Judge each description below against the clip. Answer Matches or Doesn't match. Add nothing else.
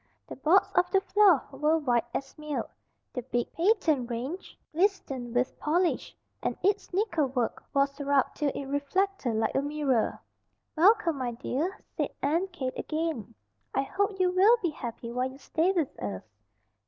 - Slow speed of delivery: Doesn't match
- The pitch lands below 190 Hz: Doesn't match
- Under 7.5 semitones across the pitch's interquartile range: Matches